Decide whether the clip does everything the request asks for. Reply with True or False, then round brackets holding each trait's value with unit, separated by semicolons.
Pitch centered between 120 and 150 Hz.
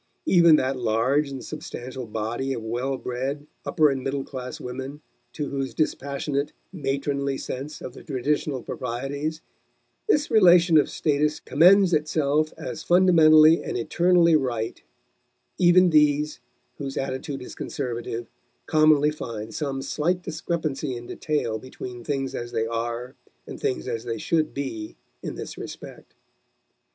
True (140 Hz)